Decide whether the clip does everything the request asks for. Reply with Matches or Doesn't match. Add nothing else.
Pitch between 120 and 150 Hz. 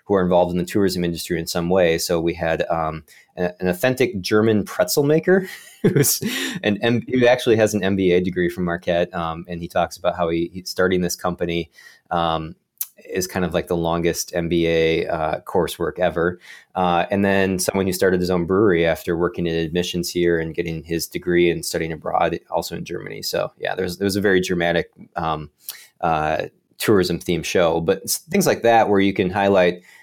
Doesn't match